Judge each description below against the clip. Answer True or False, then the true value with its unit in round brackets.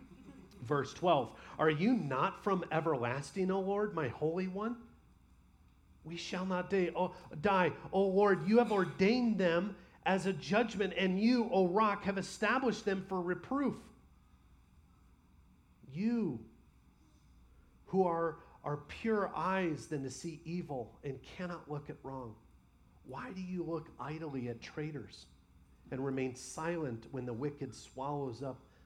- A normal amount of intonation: False (6.5 semitones)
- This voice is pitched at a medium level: True (165 Hz)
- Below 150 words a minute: True (135 wpm)